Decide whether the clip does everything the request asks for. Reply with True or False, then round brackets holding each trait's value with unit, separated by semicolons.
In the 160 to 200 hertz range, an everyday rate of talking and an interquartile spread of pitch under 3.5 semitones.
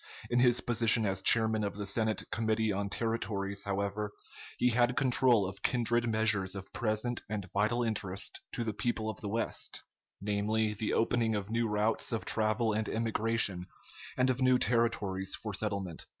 False (110 Hz; 165 wpm; 2.4 semitones)